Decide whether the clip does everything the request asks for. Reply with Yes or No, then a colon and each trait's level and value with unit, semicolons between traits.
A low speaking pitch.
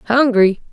No: high, 230 Hz